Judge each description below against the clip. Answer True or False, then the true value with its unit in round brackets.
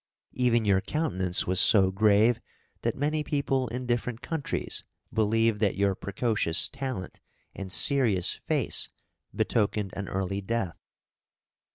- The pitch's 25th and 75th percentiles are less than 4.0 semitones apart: False (4.3 semitones)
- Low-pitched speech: True (110 Hz)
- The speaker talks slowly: True (125 wpm)